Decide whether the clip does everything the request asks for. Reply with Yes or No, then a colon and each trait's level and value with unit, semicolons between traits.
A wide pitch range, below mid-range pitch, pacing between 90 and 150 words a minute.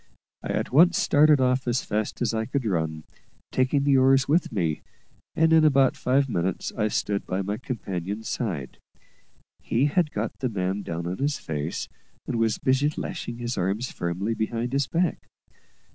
No: wide, 5.9 semitones; low, 120 Hz; average, 175 wpm